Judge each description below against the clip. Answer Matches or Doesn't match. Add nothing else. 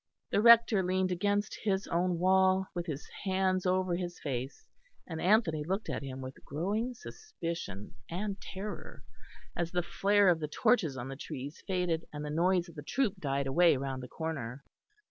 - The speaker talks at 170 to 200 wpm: Matches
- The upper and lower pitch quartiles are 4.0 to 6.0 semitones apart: Matches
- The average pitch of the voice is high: Doesn't match